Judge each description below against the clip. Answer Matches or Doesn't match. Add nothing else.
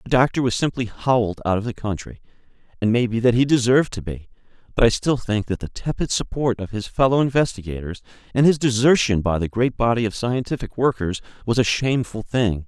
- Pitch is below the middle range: Matches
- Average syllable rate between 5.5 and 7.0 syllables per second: Matches